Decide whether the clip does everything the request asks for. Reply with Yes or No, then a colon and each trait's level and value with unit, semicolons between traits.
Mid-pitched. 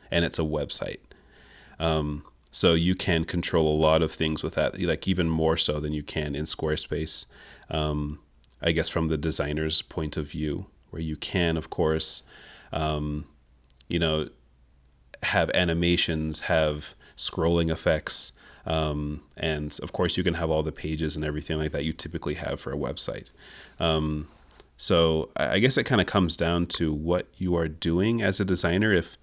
No: very low, 80 Hz